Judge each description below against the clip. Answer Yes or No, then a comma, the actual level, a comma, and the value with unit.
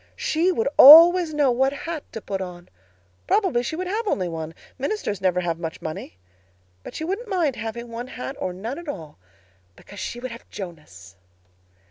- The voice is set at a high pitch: Yes, high, 240 Hz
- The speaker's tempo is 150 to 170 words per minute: No, average, 180 wpm